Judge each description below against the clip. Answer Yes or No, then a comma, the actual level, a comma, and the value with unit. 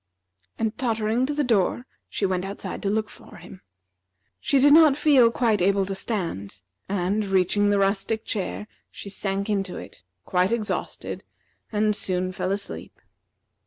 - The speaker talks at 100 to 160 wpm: Yes, average, 150 wpm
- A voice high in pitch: Yes, high, 205 Hz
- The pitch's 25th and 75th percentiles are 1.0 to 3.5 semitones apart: Yes, average, 2.7 semitones